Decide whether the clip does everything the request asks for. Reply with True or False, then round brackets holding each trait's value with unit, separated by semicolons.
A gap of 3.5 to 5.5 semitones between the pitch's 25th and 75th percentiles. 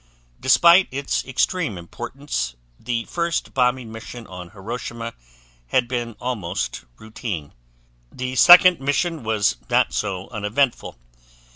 True (4.4 semitones)